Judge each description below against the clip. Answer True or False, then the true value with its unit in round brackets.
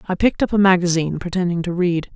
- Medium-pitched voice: True (180 Hz)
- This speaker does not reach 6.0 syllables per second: False (7.1 syllables/s)